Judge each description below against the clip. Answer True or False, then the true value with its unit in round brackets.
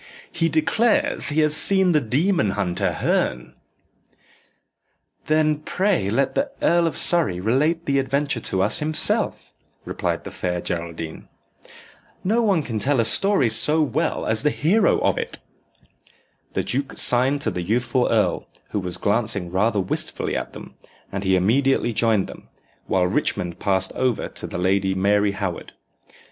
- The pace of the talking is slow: False (155 wpm)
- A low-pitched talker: True (120 Hz)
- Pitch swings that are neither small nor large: False (8.1 semitones)